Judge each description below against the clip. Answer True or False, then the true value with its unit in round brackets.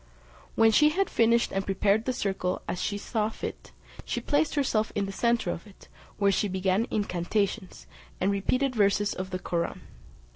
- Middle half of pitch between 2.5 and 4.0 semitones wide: True (3.3 semitones)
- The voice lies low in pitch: False (205 Hz)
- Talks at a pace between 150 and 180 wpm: True (175 wpm)